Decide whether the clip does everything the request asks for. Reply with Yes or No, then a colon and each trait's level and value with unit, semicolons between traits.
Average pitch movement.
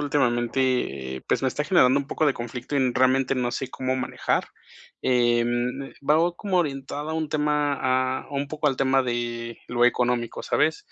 Yes: average, 3.2 semitones